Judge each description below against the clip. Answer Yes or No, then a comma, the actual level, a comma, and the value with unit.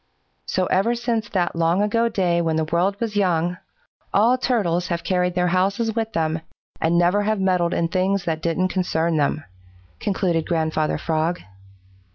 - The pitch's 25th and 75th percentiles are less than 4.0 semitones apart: Yes, average, 3.4 semitones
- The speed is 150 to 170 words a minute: Yes, average, 165 wpm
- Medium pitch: Yes, medium, 180 Hz